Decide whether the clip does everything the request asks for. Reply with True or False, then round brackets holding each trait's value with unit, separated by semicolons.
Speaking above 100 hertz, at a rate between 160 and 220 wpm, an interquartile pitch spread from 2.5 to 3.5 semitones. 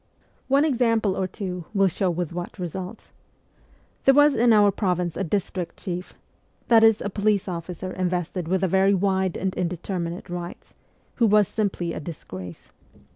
True (190 Hz; 170 wpm; 2.9 semitones)